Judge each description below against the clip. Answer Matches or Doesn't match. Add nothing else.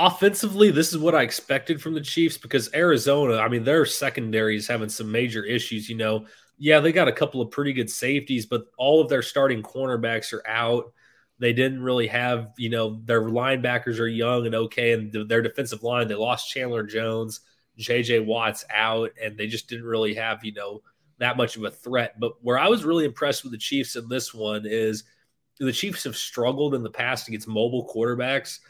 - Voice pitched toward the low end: Matches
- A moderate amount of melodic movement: Matches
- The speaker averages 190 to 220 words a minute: Matches